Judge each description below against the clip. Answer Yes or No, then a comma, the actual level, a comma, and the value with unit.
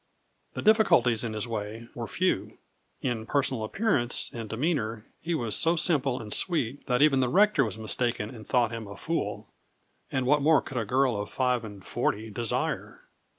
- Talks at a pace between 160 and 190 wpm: Yes, average, 180 wpm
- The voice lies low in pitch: Yes, low, 125 Hz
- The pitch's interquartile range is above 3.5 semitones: Yes, average, 4.5 semitones